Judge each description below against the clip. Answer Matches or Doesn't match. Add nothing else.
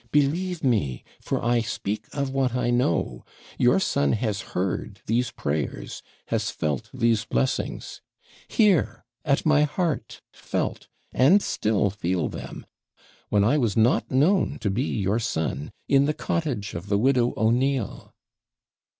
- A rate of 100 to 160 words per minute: Matches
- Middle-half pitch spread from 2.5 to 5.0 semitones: Doesn't match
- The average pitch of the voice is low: Matches